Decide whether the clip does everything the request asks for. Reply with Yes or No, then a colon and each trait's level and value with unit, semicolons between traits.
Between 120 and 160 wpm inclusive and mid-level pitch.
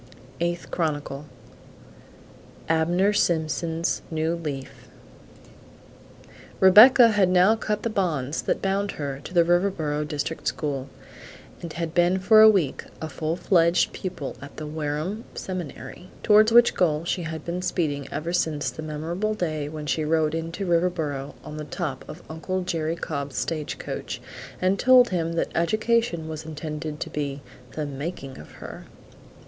Yes: average, 145 wpm; medium, 165 Hz